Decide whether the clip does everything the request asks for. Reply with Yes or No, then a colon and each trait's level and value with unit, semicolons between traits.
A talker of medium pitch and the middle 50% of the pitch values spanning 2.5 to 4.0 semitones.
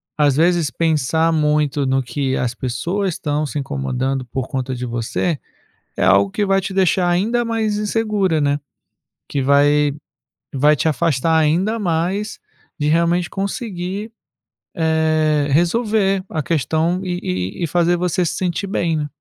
No: medium, 160 Hz; average, 4.5 semitones